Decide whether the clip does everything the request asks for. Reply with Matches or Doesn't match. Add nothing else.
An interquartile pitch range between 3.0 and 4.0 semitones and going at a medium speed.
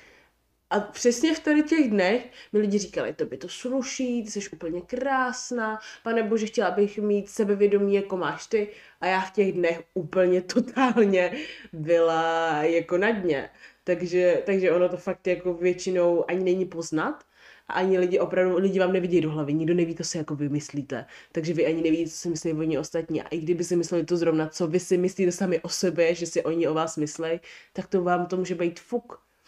Doesn't match